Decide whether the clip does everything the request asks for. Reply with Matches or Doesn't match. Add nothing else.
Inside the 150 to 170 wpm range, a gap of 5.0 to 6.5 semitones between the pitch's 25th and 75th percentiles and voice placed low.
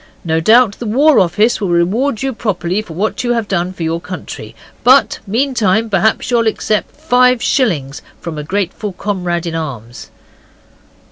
Doesn't match